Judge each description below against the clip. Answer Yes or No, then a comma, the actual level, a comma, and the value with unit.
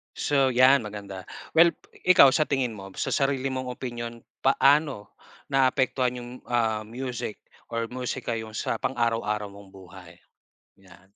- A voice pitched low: Yes, low, 120 Hz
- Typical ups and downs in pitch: Yes, average, 4.0 semitones